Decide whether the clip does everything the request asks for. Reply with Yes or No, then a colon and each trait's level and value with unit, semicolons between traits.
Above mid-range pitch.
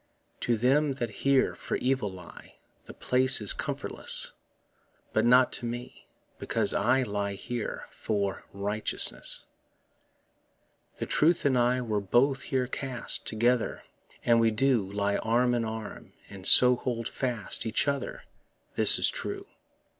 No: low, 120 Hz